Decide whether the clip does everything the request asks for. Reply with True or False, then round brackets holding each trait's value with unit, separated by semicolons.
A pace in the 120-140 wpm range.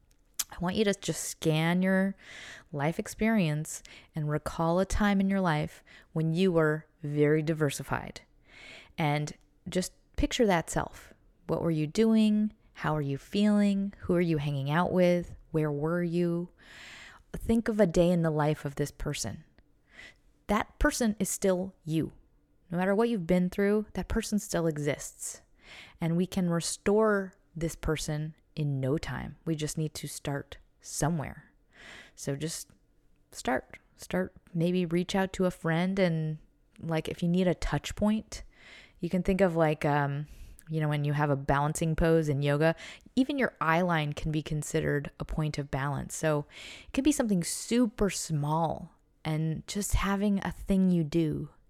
False (165 wpm)